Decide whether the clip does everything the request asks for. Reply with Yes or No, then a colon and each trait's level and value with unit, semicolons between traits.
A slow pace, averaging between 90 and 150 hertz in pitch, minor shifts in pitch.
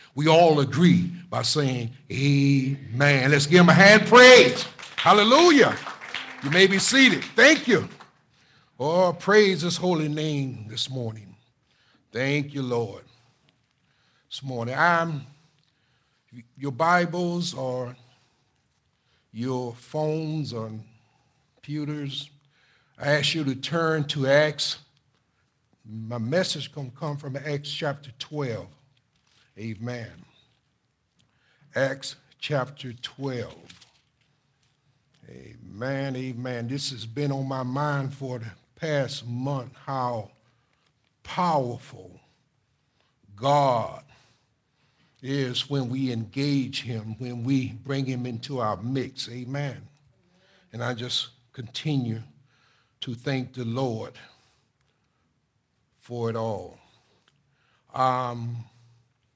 No: slow, 100 wpm; low, 135 Hz; average, 3.1 semitones